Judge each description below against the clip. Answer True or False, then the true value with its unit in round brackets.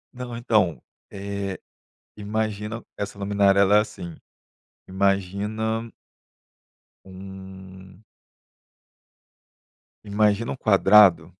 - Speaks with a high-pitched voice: False (100 Hz)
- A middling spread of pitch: False (2.0 semitones)